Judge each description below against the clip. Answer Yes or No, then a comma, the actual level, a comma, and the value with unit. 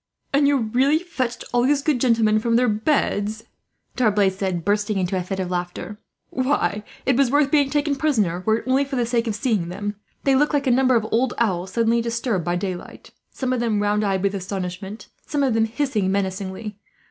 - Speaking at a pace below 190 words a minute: No, fast, 205 wpm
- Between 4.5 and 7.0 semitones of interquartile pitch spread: Yes, average, 4.8 semitones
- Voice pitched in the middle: No, high, 225 Hz